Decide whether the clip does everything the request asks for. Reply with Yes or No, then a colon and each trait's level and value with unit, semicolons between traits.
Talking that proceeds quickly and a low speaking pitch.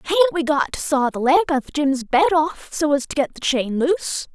No: fast, 250 wpm; very high, 300 Hz